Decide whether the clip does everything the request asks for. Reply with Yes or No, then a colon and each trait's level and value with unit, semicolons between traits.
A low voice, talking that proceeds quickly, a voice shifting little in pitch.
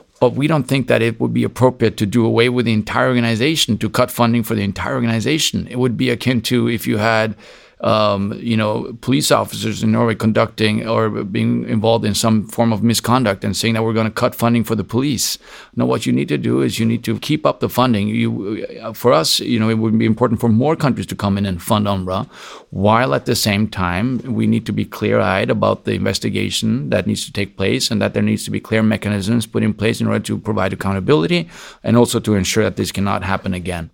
Yes: low, 110 Hz; fast, 235 wpm; narrow, 2.3 semitones